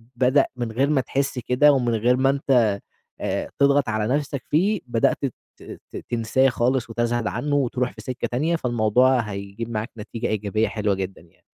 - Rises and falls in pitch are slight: No, average, 3.4 semitones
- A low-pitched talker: Yes, low, 120 Hz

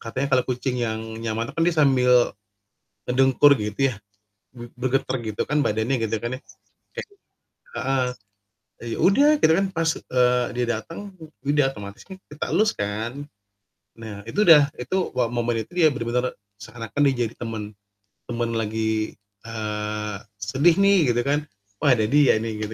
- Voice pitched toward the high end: No, low, 125 Hz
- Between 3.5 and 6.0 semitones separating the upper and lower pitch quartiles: Yes, average, 4.3 semitones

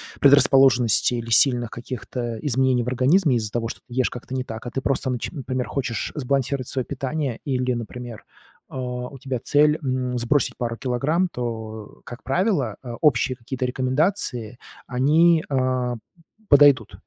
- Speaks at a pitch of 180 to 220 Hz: No, low, 130 Hz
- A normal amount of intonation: No, narrow, 2.3 semitones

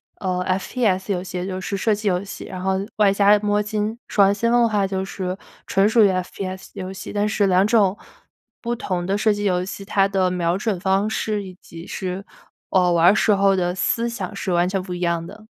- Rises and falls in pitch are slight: Yes, narrow, 2.1 semitones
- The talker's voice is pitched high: Yes, high, 195 Hz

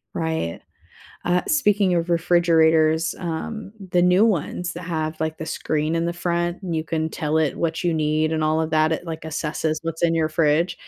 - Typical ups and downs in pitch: No, narrow, 1.7 semitones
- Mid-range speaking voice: Yes, medium, 165 Hz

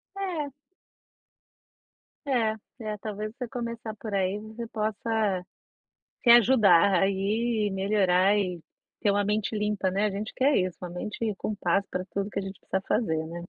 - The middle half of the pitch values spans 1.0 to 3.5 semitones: Yes, narrow, 2.4 semitones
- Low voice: No, high, 210 Hz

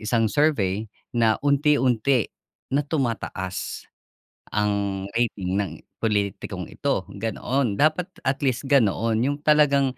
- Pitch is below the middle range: Yes, low, 115 Hz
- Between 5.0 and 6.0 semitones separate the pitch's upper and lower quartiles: Yes, average, 5.3 semitones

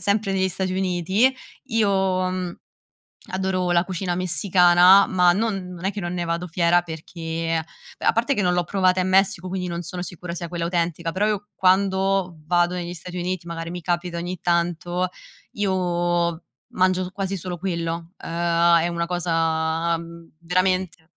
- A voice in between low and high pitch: Yes, medium, 180 Hz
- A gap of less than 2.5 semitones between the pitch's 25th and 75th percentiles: Yes, narrow, 1.7 semitones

